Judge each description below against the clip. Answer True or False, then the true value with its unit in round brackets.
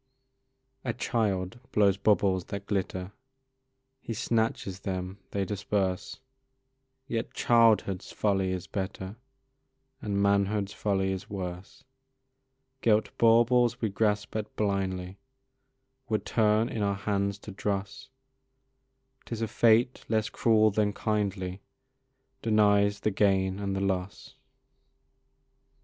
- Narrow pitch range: True (2.1 semitones)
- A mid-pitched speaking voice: False (100 Hz)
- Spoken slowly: True (110 wpm)